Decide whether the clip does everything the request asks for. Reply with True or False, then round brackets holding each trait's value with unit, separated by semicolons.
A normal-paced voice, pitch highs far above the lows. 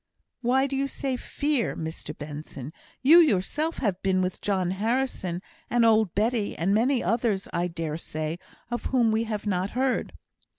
True (165 wpm; 5.9 semitones)